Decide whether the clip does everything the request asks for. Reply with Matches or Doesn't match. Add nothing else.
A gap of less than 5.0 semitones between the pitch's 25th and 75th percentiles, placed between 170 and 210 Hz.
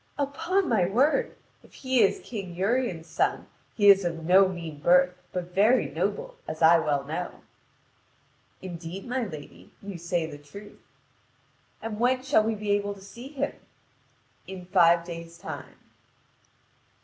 Doesn't match